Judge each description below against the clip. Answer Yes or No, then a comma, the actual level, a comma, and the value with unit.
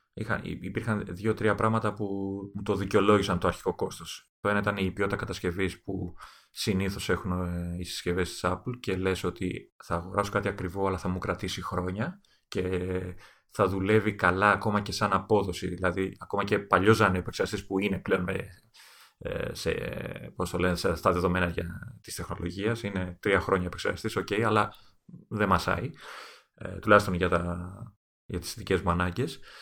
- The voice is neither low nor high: No, very low, 95 Hz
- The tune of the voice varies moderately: No, narrow, 2.3 semitones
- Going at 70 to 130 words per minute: No, average, 150 wpm